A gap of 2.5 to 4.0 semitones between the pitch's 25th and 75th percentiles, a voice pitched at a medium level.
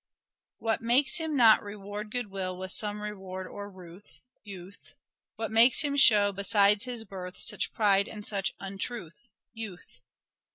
No: average, 2.8 semitones; high, 205 Hz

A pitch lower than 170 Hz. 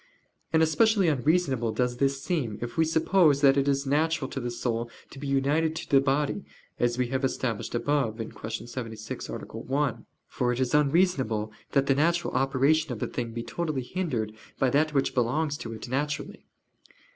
Yes: low, 135 Hz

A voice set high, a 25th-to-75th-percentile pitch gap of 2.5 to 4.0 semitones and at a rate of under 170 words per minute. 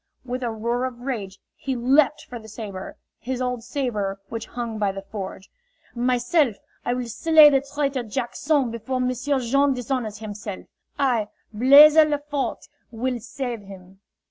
Yes: high, 245 Hz; average, 3.7 semitones; average, 155 wpm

